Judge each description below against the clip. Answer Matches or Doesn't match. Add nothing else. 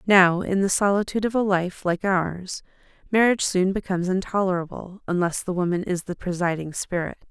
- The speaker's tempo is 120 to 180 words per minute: Matches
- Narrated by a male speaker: Doesn't match